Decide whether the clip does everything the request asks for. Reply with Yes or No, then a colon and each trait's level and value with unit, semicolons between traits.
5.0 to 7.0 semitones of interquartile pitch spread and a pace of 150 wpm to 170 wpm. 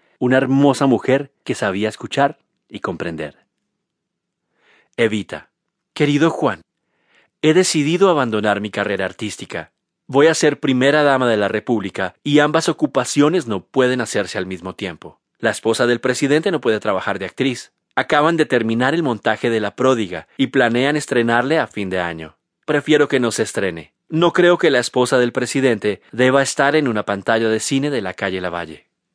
Yes: wide, 5.5 semitones; average, 165 wpm